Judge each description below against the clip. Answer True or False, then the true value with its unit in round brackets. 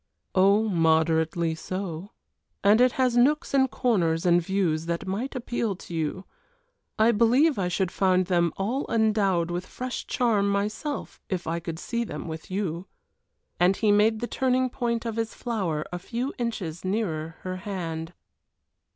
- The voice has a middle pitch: False (195 Hz)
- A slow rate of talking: False (160 wpm)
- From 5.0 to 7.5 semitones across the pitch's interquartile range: True (5.3 semitones)